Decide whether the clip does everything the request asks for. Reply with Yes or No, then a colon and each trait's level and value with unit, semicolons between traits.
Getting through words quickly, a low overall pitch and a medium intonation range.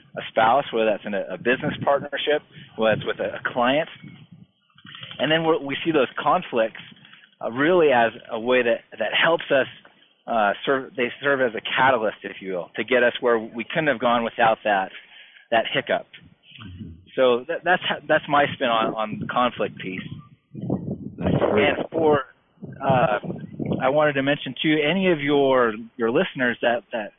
No: average, 175 wpm; low, 130 Hz; average, 4.4 semitones